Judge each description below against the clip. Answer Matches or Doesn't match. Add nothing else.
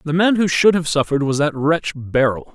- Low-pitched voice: Doesn't match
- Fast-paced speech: Matches